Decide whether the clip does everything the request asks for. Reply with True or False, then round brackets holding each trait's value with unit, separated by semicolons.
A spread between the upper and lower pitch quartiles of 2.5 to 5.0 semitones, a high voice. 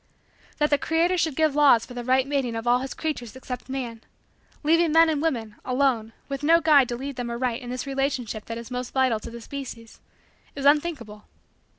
True (3.5 semitones; 260 Hz)